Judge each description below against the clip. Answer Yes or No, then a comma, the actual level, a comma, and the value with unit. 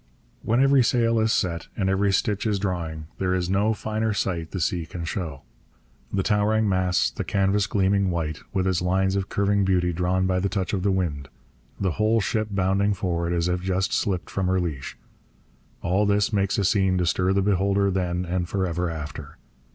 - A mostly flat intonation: Yes, narrow, 2.2 semitones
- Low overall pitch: Yes, very low, 95 Hz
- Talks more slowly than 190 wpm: No, average, 200 wpm